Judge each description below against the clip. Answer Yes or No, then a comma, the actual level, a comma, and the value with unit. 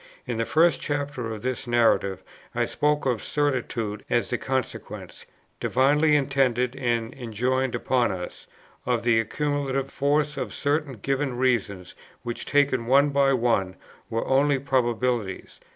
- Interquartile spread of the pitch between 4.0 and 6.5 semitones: No, average, 3.3 semitones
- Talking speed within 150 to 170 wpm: No, slow, 135 wpm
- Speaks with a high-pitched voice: No, low, 130 Hz